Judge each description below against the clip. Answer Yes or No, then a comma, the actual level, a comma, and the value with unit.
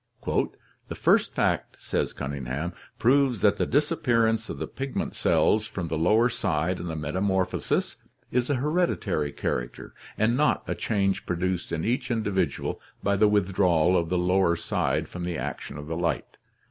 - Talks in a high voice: No, very low, 95 Hz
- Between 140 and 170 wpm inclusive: Yes, average, 165 wpm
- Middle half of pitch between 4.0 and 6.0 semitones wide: Yes, average, 5.2 semitones